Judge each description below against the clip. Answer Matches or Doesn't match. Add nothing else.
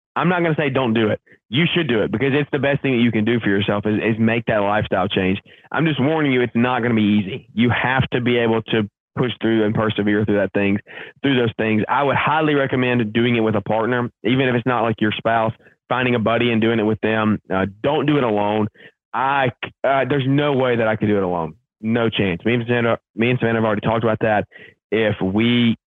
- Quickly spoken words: Matches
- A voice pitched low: Matches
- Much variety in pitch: Doesn't match